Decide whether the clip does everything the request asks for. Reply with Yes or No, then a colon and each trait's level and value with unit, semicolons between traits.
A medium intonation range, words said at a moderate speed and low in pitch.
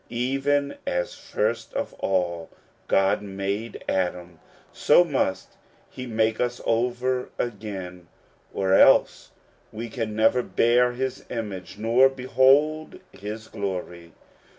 No: average, 4.7 semitones; slow, 110 wpm; low, 115 Hz